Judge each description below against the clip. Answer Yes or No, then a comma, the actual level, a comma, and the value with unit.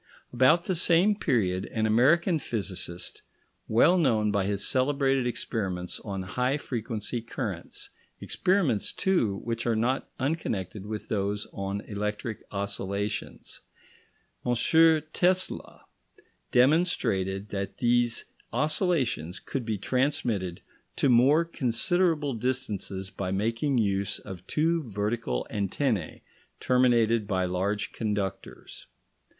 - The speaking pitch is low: Yes, low, 115 Hz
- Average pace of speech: No, slow, 105 wpm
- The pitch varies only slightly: No, average, 5.2 semitones